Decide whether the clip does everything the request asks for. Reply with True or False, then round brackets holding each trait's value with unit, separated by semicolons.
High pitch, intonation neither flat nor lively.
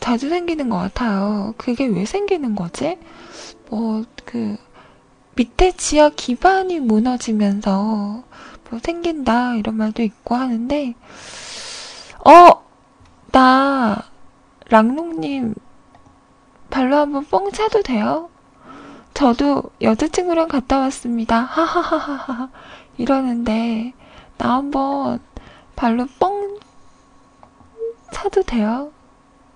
False (260 Hz; 6.0 semitones)